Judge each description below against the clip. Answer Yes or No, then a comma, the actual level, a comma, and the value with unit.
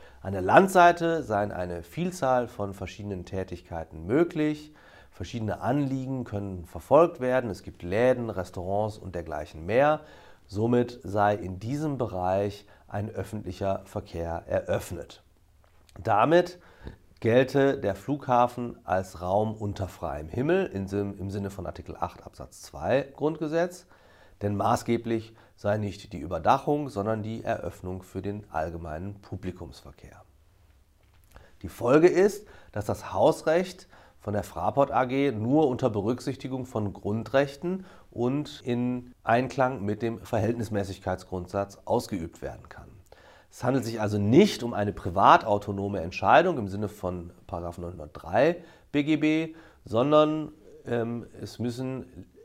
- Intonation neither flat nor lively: No, wide, 5.7 semitones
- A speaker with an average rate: No, slow, 120 wpm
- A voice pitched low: Yes, low, 105 Hz